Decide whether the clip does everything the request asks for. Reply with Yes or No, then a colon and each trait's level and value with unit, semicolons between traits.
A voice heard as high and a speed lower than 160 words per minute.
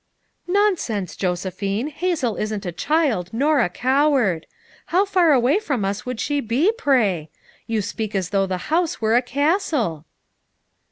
Yes: high, 240 Hz; average, 150 wpm